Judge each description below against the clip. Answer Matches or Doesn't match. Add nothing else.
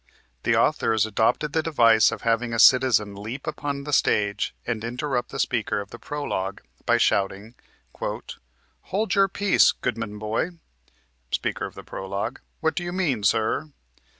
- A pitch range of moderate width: Doesn't match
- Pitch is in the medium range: Doesn't match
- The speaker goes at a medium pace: Matches